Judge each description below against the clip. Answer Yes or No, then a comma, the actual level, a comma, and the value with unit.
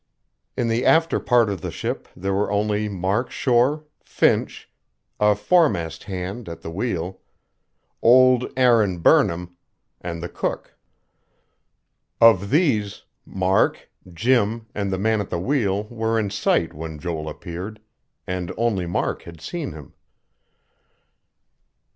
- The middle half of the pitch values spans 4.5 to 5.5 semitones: Yes, average, 4.9 semitones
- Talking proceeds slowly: Yes, slow, 130 wpm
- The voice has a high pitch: No, low, 100 Hz